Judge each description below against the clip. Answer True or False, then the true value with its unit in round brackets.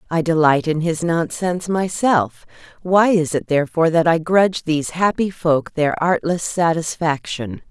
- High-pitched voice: False (165 Hz)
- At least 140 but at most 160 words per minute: True (150 wpm)